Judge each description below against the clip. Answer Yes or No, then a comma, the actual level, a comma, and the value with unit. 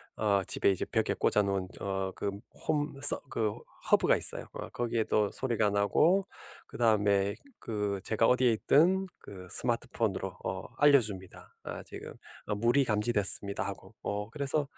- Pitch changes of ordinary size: Yes, average, 4.0 semitones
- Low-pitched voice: Yes, low, 105 Hz